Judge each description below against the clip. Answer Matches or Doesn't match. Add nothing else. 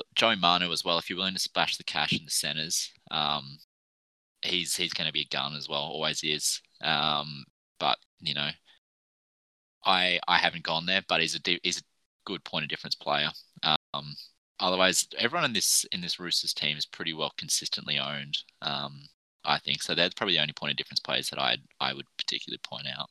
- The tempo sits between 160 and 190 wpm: Doesn't match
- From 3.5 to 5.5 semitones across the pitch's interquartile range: Doesn't match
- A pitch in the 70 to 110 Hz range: Matches